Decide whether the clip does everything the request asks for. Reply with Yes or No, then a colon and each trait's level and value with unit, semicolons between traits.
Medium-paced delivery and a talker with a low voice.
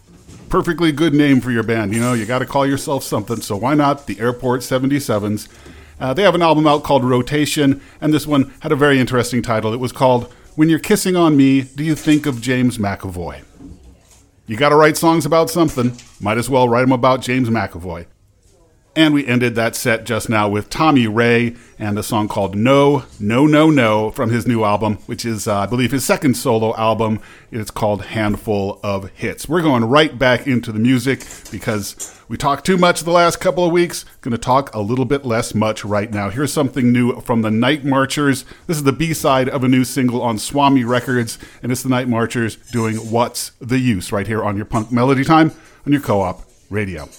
No: fast, 210 wpm; low, 125 Hz